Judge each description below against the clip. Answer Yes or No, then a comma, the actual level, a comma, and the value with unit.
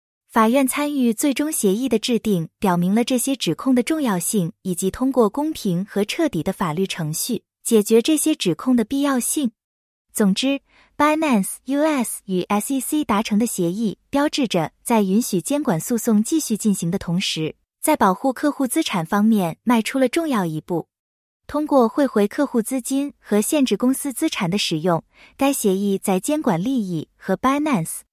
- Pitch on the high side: Yes, high, 230 Hz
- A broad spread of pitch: Yes, wide, 6.1 semitones